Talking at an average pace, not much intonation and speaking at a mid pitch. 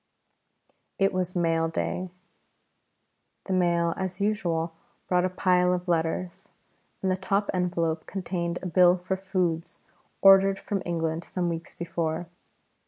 No: slow, 130 wpm; narrow, 1.8 semitones; medium, 180 Hz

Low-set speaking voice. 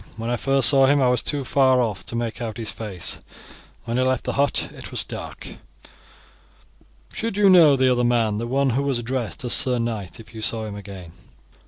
Yes: low, 120 Hz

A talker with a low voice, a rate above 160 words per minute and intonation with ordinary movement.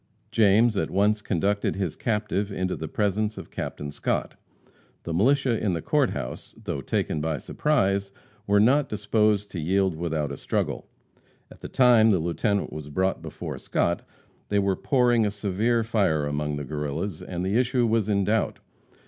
Yes: low, 100 Hz; average, 170 wpm; average, 4.2 semitones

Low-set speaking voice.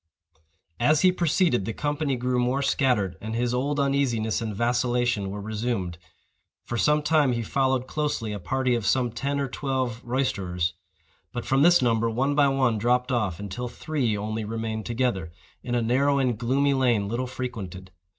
Yes: low, 125 Hz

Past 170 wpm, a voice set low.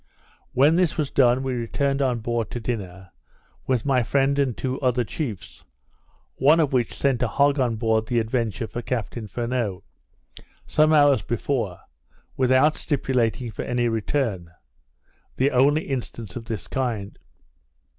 No: average, 145 wpm; low, 125 Hz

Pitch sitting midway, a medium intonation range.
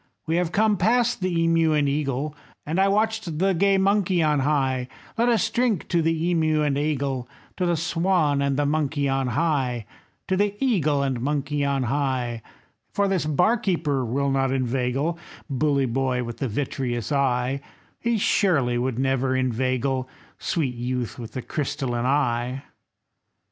Yes: medium, 145 Hz; average, 4.7 semitones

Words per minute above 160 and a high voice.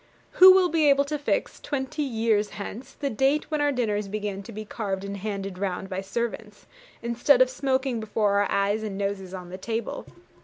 Yes: average, 195 wpm; high, 220 Hz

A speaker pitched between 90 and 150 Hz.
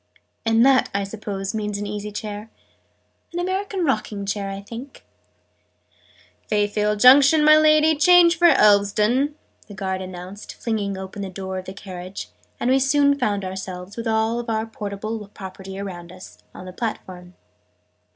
No: high, 210 Hz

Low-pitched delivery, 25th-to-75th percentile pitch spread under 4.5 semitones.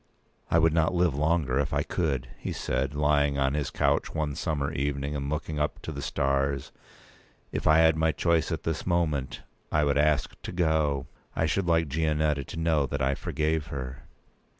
Yes: very low, 75 Hz; narrow, 2.4 semitones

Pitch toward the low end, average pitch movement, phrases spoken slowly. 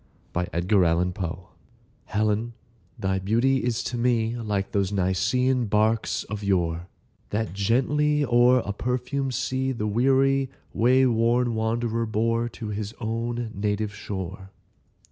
Yes: low, 110 Hz; average, 3.5 semitones; slow, 125 wpm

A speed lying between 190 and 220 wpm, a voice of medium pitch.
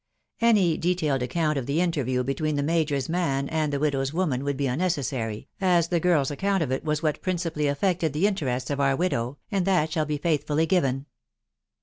Yes: average, 200 wpm; medium, 150 Hz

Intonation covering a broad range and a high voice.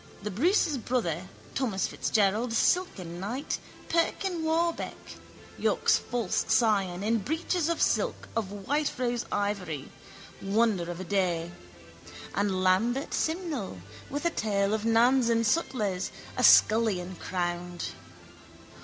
Yes: wide, 6.0 semitones; high, 215 Hz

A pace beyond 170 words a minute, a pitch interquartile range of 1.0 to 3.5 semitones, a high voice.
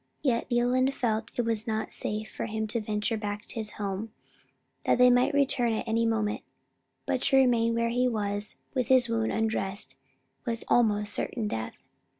Yes: average, 180 wpm; narrow, 2.5 semitones; high, 225 Hz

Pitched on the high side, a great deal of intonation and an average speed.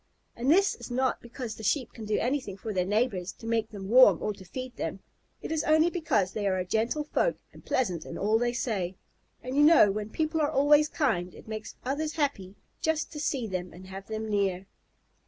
No: high, 225 Hz; wide, 6.4 semitones; fast, 220 wpm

